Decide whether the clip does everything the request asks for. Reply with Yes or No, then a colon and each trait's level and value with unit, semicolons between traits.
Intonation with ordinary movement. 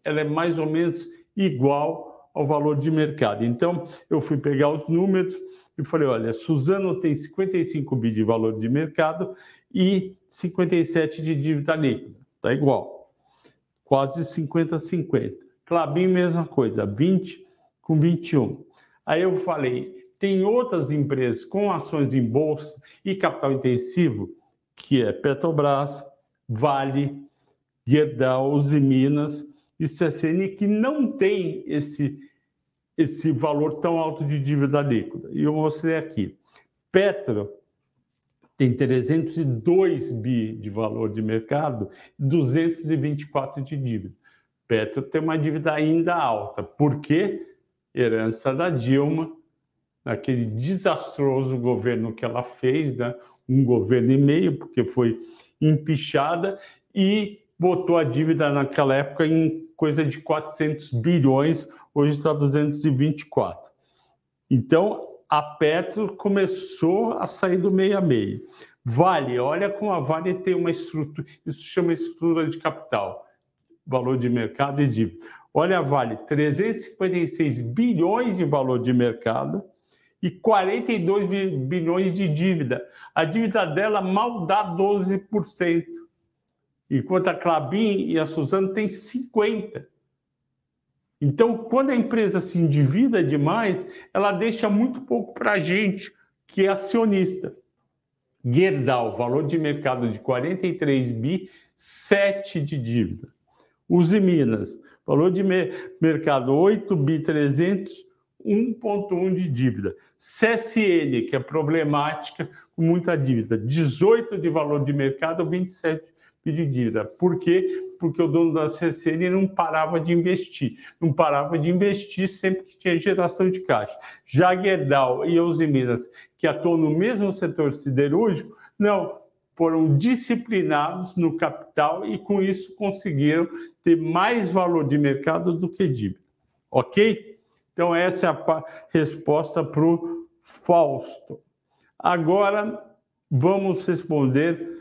Yes: average, 4.7 semitones